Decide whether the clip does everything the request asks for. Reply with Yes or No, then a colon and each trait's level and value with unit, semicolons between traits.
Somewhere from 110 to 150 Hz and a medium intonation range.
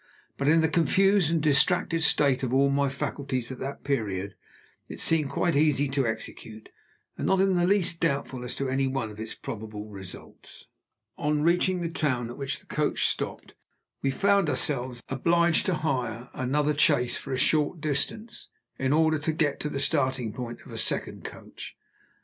Yes: medium, 140 Hz; average, 4.0 semitones